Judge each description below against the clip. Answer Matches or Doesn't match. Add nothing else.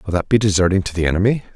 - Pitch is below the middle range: Matches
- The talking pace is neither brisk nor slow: Doesn't match